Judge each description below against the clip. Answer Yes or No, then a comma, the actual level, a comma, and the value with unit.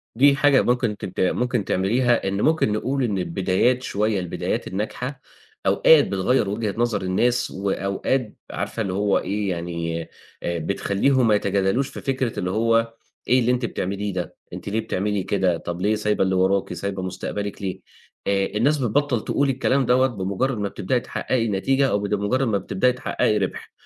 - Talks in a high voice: No, low, 105 Hz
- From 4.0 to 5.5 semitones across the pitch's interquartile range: Yes, average, 4.5 semitones